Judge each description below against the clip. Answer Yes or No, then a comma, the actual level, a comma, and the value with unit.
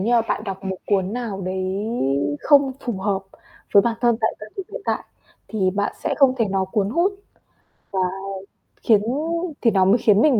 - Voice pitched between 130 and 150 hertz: No, high, 210 Hz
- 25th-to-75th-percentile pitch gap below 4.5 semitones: Yes, average, 3.8 semitones